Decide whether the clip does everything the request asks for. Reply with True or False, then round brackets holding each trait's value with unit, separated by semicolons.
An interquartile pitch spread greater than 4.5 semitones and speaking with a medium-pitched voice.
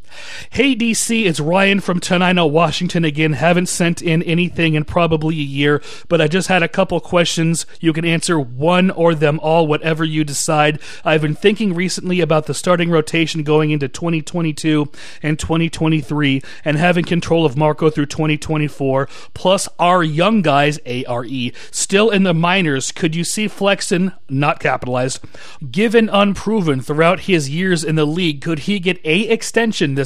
False (3.0 semitones; 165 Hz)